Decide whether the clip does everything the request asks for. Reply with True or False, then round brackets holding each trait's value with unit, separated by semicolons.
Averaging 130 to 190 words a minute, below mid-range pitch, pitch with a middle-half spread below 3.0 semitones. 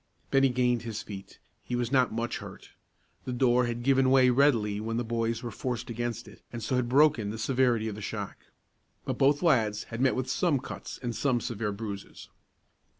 False (200 wpm; 120 Hz; 2.5 semitones)